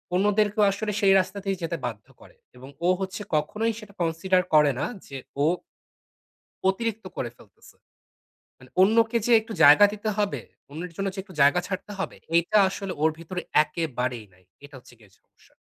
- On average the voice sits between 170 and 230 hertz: Yes, medium, 185 Hz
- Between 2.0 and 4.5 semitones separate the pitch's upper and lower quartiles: No, wide, 5.6 semitones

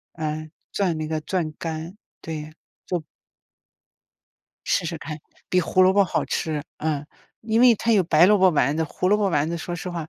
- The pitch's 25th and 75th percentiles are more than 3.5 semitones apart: No, average, 3.2 semitones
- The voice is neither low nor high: Yes, medium, 165 Hz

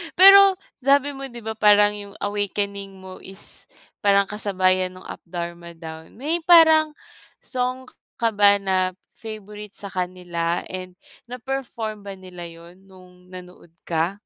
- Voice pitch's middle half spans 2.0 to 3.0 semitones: No, average, 3.8 semitones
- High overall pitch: Yes, high, 200 Hz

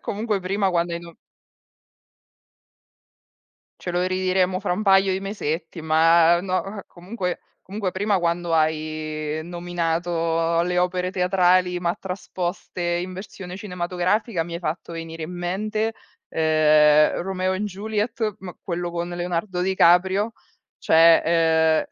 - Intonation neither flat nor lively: No, narrow, 2.1 semitones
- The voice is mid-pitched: Yes, medium, 180 Hz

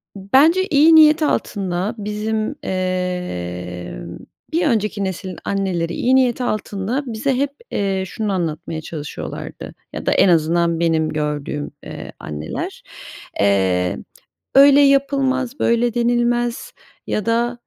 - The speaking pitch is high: Yes, high, 205 Hz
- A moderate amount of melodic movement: No, wide, 7.1 semitones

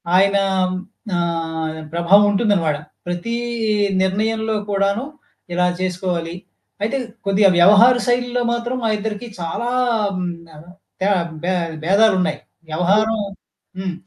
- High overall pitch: Yes, high, 200 Hz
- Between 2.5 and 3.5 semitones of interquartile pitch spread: No, average, 4.0 semitones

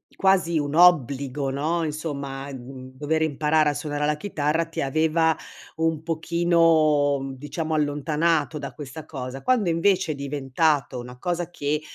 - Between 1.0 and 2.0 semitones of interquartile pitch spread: No, average, 2.7 semitones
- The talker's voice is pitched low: No, medium, 150 Hz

